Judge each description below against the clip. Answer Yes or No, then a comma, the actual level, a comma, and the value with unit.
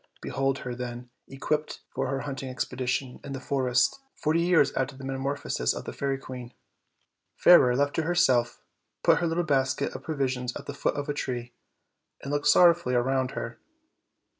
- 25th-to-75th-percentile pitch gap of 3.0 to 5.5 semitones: No, narrow, 2.4 semitones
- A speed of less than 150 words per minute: No, average, 185 wpm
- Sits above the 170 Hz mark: No, low, 135 Hz